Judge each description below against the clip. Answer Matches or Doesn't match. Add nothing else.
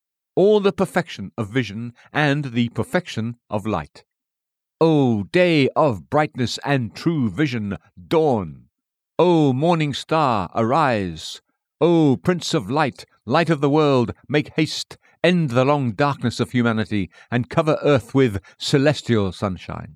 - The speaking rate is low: Matches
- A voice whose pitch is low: Matches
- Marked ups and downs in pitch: Matches